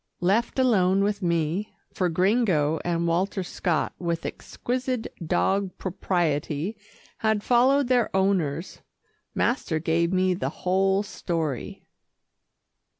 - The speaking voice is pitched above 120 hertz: Yes, medium, 185 Hz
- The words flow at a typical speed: No, slow, 105 wpm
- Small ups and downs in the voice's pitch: No, average, 3.8 semitones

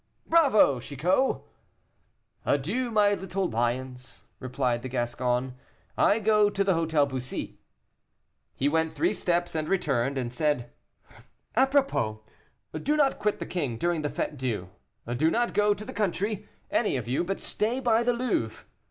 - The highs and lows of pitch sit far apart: Yes, wide, 8.6 semitones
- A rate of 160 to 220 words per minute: No, average, 150 wpm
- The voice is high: No, medium, 165 Hz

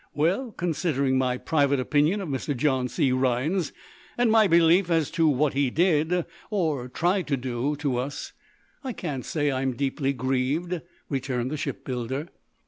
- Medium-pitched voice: Yes, medium, 145 Hz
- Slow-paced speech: No, average, 155 wpm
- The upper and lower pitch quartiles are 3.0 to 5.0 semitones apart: Yes, average, 4.4 semitones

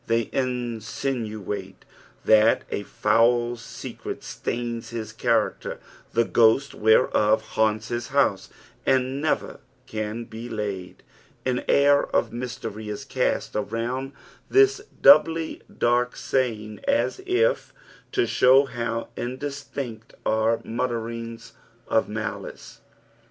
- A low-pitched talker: Yes, low, 115 Hz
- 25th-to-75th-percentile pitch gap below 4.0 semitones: Yes, average, 2.9 semitones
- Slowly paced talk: Yes, slow, 110 wpm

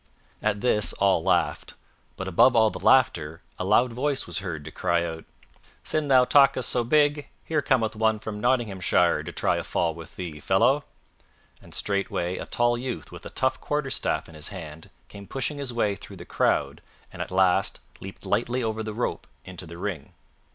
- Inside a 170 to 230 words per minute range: Yes, average, 185 wpm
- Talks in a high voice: No, low, 105 Hz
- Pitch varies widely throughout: Yes, wide, 5.8 semitones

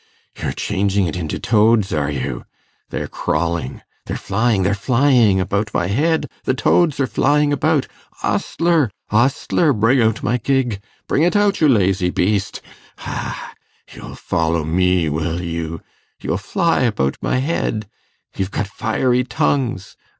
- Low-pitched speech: Yes, low, 105 Hz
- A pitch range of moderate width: No, wide, 6.5 semitones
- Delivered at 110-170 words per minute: Yes, average, 145 wpm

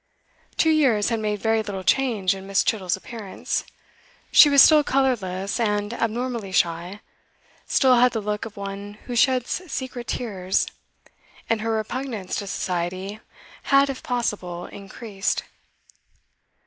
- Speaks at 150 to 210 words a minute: No, slow, 135 wpm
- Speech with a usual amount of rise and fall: Yes, average, 4.0 semitones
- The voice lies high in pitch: Yes, high, 215 Hz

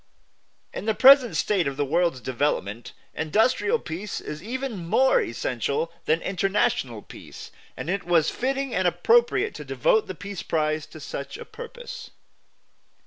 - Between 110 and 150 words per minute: Yes, average, 145 wpm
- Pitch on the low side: No, medium, 180 Hz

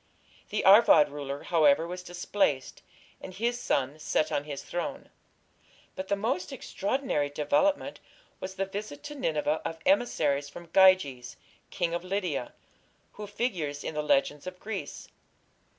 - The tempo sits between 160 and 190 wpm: No, average, 140 wpm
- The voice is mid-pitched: Yes, medium, 175 Hz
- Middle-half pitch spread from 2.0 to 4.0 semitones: No, wide, 5.5 semitones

